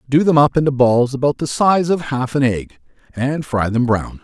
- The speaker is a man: Yes, male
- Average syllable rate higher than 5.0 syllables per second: No, 4.9 syllables/s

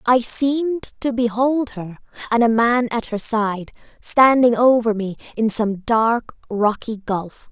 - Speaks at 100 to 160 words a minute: Yes, average, 150 wpm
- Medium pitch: No, high, 230 Hz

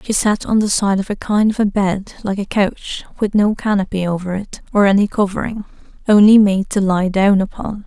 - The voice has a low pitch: No, high, 200 Hz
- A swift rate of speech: Yes, fast, 215 wpm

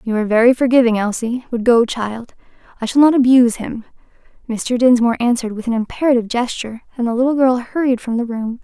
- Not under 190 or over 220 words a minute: Yes, average, 195 wpm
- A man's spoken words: No, female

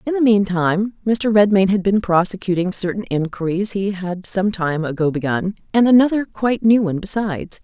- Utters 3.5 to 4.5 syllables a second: No, 5.4 syllables/s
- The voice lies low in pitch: No, high, 195 Hz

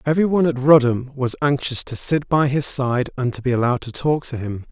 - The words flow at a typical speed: No, fast, 230 wpm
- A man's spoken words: Yes, male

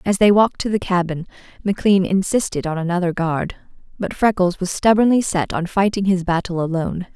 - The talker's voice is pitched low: No, medium, 185 Hz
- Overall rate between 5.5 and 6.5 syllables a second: Yes, 5.8 syllables/s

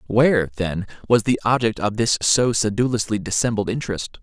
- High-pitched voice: No, low, 110 Hz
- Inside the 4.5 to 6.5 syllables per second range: Yes, 5.5 syllables/s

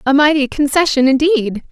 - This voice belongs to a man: No, female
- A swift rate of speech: No, average, 140 wpm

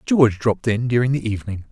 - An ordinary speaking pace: No, fast, 210 wpm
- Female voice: No, male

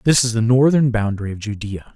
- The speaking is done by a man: Yes, male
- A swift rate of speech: Yes, fast, 215 wpm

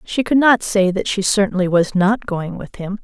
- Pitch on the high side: Yes, high, 200 Hz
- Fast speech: Yes, fast, 235 wpm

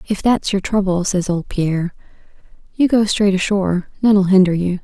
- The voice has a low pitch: No, high, 190 Hz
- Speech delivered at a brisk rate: No, average, 175 wpm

